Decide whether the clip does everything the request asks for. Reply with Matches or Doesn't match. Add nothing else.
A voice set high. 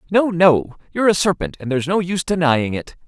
Doesn't match